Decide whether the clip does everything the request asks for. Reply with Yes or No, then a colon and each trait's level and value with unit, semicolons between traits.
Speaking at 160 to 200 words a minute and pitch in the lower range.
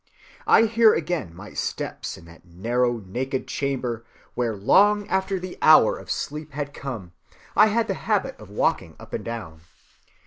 Yes: average, 165 wpm; low, 130 Hz